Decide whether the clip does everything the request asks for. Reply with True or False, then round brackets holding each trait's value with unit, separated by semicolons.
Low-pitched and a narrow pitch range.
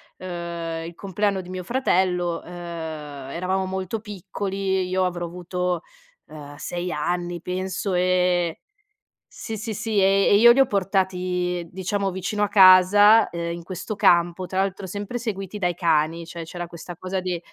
False (185 Hz; 2.1 semitones)